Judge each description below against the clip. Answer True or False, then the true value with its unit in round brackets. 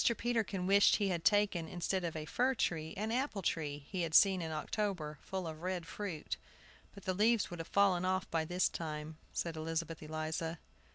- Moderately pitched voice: True (175 Hz)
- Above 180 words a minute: True (190 wpm)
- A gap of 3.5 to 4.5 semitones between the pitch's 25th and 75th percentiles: True (3.9 semitones)